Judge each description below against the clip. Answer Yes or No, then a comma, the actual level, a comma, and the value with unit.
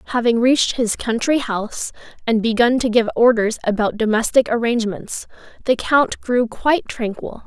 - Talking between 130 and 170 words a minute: Yes, average, 145 wpm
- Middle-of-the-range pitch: No, high, 235 Hz